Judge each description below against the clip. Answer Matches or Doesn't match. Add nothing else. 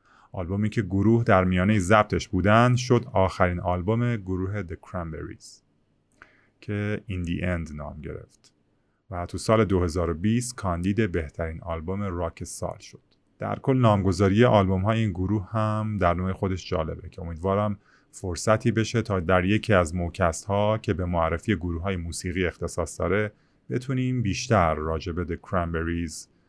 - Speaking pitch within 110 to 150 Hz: Doesn't match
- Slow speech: Doesn't match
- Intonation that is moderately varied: Matches